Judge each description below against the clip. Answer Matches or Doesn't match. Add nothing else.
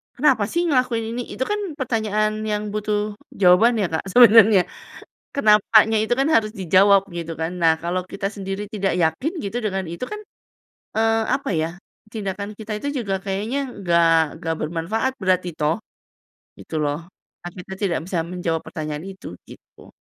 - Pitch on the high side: Matches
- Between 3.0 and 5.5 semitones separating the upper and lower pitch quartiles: Matches